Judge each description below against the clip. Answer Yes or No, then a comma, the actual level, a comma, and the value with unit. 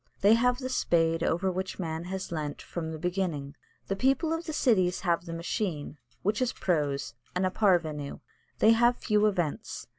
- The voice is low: No, medium, 180 Hz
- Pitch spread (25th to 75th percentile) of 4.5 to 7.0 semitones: Yes, average, 4.8 semitones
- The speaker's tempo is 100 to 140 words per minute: No, average, 180 wpm